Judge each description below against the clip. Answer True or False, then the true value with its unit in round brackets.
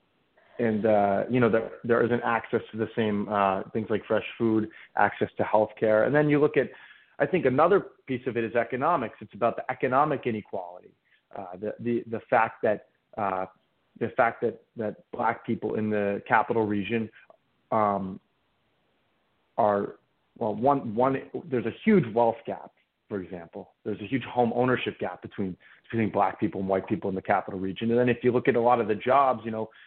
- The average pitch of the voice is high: False (115 Hz)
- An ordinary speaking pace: True (195 wpm)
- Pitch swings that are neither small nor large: True (3.1 semitones)